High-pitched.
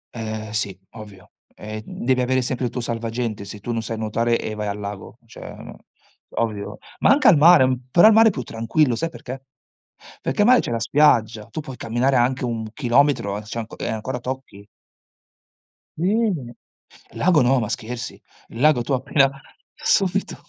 No: low, 120 Hz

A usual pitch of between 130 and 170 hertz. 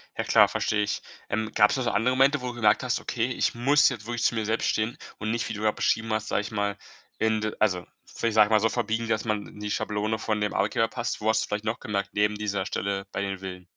No: low, 110 Hz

